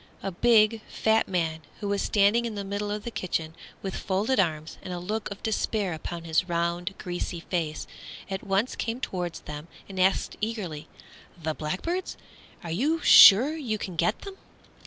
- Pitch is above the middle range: Yes, high, 195 Hz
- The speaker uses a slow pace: No, average, 175 wpm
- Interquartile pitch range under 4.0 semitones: No, average, 4.3 semitones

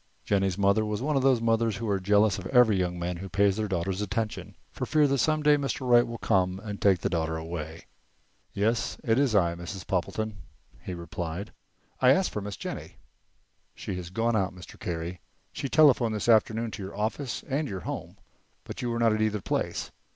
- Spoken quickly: Yes, fast, 210 wpm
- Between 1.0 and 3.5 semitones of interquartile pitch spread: No, average, 4.2 semitones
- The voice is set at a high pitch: No, low, 105 Hz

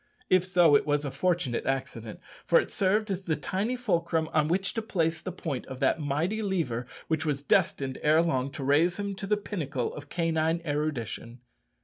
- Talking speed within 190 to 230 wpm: Yes, average, 195 wpm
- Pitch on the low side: No, medium, 160 Hz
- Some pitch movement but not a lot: Yes, average, 4.7 semitones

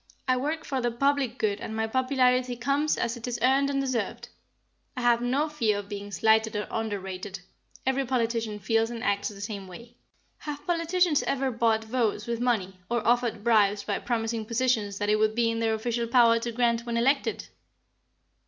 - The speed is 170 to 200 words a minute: Yes, average, 190 wpm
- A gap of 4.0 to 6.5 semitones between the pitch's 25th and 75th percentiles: No, average, 2.8 semitones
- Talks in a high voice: Yes, high, 235 Hz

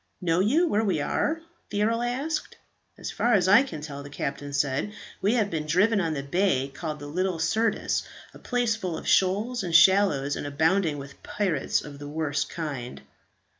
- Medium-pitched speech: Yes, medium, 175 Hz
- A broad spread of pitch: Yes, wide, 6.4 semitones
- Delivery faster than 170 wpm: Yes, average, 190 wpm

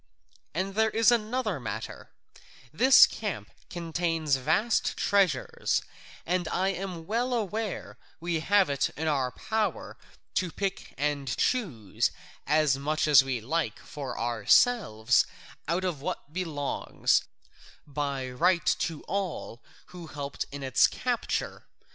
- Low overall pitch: No, medium, 165 Hz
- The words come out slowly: Yes, slow, 125 wpm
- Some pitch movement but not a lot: No, wide, 5.8 semitones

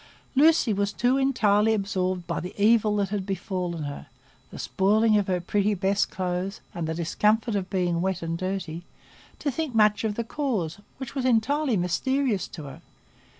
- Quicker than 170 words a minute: No, average, 165 wpm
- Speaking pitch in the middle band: No, high, 200 Hz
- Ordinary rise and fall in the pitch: Yes, average, 3.9 semitones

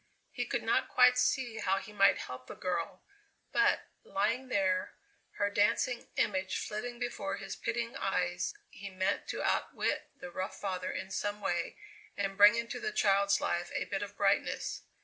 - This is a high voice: Yes, high, 200 Hz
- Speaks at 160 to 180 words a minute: Yes, average, 170 wpm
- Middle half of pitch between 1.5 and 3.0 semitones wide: No, average, 3.5 semitones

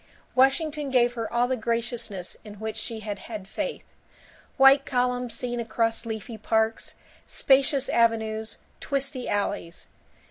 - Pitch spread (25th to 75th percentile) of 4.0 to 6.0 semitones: No, average, 2.8 semitones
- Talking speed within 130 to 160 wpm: Yes, slow, 135 wpm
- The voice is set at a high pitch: Yes, high, 235 Hz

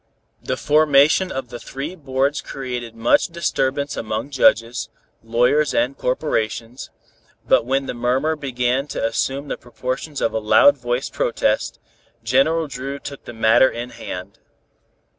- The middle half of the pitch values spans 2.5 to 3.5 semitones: Yes, average, 3.0 semitones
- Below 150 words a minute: Yes, average, 140 wpm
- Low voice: Yes, low, 130 Hz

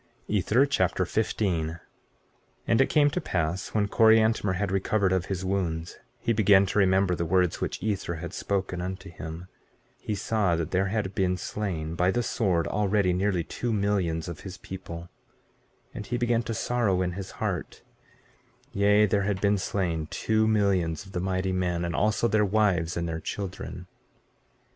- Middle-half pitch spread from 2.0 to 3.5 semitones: Yes, average, 2.9 semitones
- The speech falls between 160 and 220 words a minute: Yes, average, 170 wpm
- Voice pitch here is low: Yes, very low, 95 Hz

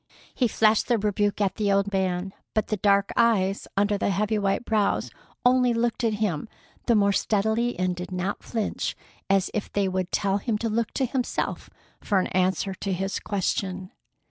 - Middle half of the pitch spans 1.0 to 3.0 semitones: Yes, narrow, 2.4 semitones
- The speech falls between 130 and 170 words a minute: No, average, 185 wpm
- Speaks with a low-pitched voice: No, high, 205 Hz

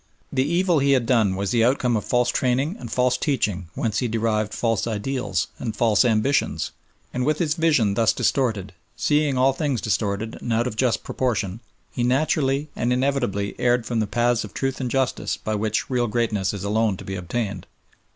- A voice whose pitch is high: No, low, 120 Hz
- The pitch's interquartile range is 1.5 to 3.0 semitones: No, average, 3.7 semitones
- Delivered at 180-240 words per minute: Yes, average, 190 wpm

